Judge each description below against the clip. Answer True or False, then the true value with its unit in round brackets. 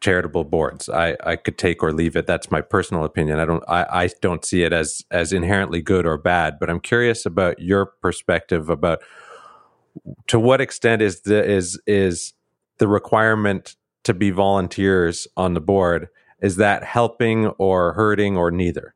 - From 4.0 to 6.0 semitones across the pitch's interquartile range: False (3.3 semitones)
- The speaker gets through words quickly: False (175 wpm)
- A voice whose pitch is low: True (95 Hz)